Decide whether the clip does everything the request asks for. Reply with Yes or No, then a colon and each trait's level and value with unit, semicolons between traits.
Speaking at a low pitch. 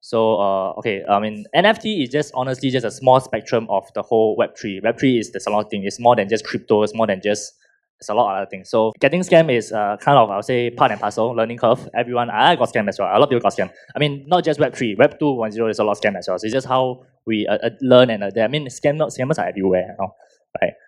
Yes: low, 115 Hz